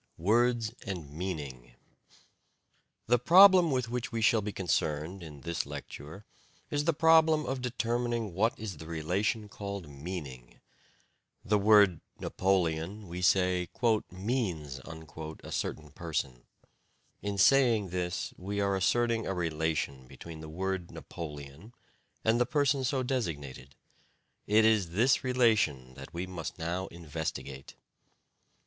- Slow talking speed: Yes, slow, 125 wpm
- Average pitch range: No, wide, 6.3 semitones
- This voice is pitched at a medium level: No, very low, 95 Hz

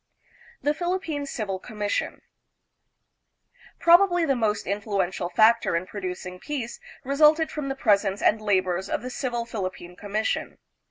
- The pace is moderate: No, slow, 125 wpm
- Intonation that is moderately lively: No, wide, 6.5 semitones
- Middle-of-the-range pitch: No, high, 220 Hz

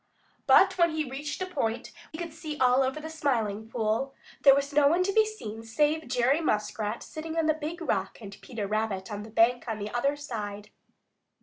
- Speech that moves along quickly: Yes, fast, 210 wpm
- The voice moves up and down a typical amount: No, wide, 6.1 semitones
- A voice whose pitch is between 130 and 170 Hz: No, very high, 270 Hz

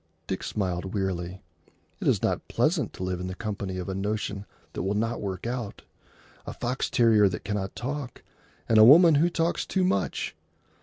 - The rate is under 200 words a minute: Yes, average, 185 wpm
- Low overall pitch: Yes, low, 105 Hz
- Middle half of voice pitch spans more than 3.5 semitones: Yes, average, 4.1 semitones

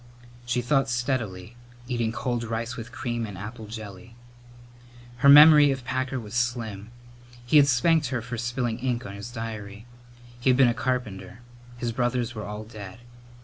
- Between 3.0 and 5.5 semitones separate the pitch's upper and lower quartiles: No, narrow, 2.4 semitones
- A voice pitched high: No, low, 120 Hz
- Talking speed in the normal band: Yes, average, 165 wpm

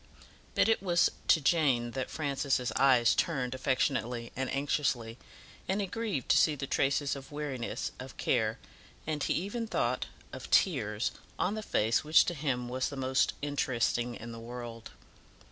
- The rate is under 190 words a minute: Yes, average, 160 wpm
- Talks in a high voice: No, low, 135 Hz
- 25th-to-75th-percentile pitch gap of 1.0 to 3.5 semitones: No, average, 3.9 semitones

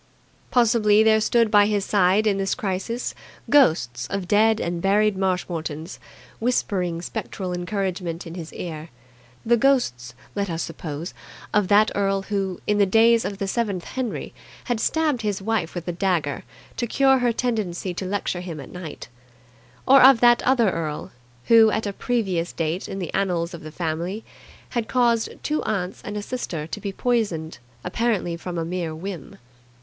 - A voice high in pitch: Yes, high, 195 Hz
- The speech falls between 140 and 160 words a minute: No, average, 170 wpm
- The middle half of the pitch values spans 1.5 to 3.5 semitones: No, average, 4.4 semitones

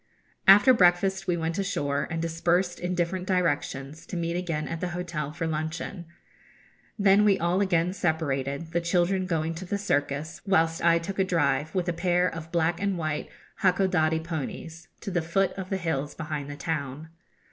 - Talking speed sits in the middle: Yes, average, 180 wpm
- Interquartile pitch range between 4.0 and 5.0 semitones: No, narrow, 2.5 semitones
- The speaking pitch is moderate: Yes, medium, 170 Hz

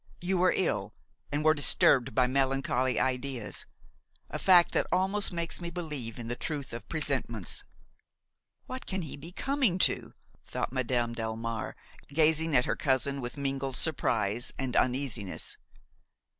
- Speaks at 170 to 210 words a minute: No, average, 145 wpm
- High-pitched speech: No, low, 135 Hz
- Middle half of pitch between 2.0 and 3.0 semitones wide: No, average, 5.1 semitones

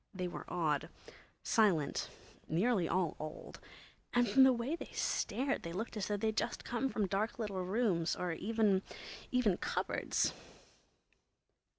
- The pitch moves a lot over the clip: No, average, 4.8 semitones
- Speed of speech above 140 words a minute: No, slow, 135 wpm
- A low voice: No, high, 205 Hz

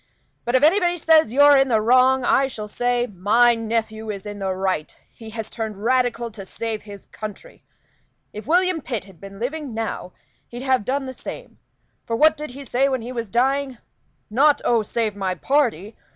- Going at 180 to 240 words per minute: Yes, average, 190 wpm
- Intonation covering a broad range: No, average, 4.1 semitones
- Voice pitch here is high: Yes, high, 235 Hz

